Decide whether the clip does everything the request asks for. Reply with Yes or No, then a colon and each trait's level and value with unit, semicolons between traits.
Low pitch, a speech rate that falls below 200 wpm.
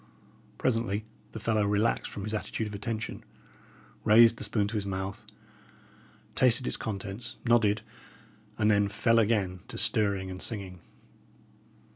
Yes: low, 105 Hz; slow, 135 wpm